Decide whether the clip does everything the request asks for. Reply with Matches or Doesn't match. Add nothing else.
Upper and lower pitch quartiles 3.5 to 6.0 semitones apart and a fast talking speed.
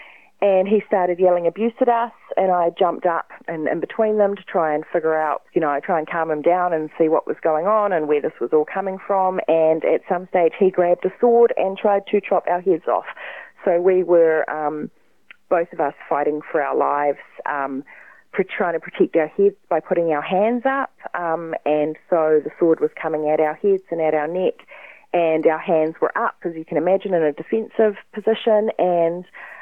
Matches